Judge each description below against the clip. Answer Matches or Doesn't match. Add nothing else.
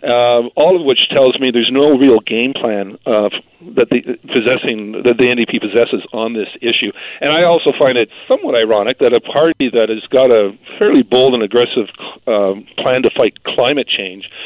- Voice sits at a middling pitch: Doesn't match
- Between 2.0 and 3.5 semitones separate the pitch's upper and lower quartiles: Doesn't match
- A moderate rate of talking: Matches